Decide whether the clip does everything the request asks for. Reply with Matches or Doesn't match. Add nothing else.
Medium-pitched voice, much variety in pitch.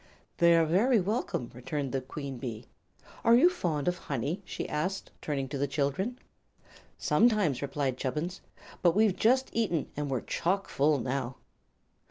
Matches